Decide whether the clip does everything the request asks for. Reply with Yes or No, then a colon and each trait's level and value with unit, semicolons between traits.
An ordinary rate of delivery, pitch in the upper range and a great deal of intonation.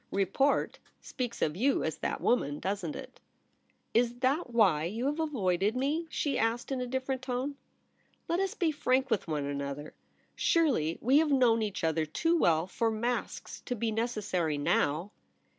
Yes: average, 185 wpm; high, 235 Hz; wide, 7.2 semitones